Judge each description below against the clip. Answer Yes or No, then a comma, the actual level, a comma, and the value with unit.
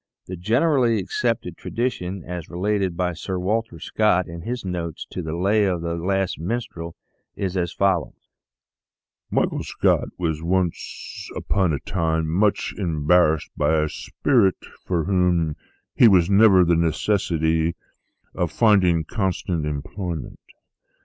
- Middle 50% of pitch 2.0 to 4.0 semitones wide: Yes, average, 3.1 semitones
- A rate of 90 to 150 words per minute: Yes, average, 140 wpm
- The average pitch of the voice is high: No, very low, 90 Hz